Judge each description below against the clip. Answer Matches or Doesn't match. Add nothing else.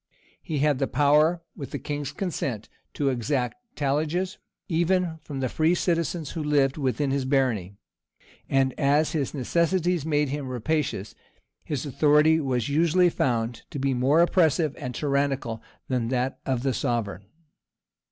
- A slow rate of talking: Doesn't match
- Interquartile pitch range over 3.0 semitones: Matches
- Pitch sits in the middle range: Matches